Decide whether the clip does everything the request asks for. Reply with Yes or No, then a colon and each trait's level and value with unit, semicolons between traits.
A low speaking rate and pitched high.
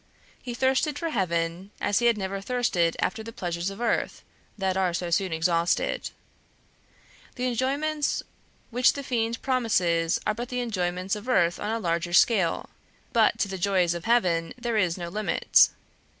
No: average, 165 wpm; high, 200 Hz